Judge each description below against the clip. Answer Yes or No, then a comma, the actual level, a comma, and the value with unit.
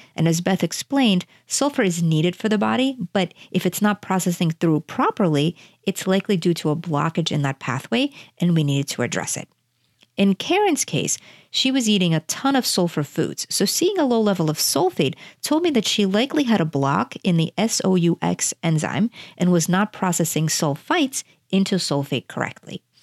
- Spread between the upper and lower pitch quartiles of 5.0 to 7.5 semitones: Yes, average, 5.3 semitones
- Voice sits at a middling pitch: Yes, medium, 180 Hz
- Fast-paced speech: No, average, 180 wpm